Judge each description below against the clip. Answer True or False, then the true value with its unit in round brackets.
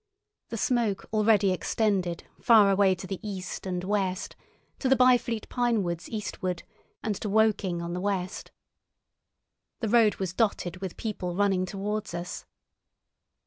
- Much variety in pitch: False (3.0 semitones)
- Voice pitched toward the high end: True (200 Hz)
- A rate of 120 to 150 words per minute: True (140 wpm)